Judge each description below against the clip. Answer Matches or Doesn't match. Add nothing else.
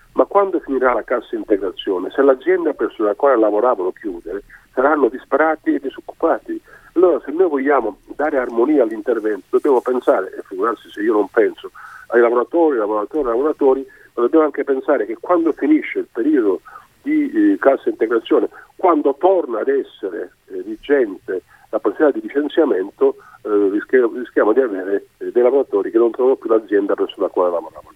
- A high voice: Matches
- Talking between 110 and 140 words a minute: Doesn't match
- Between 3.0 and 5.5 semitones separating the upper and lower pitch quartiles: Matches